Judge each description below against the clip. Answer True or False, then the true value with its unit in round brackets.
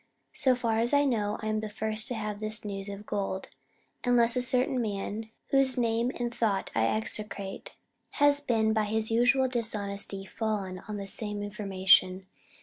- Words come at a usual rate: True (165 wpm)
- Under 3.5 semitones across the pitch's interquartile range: True (2.9 semitones)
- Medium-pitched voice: False (215 Hz)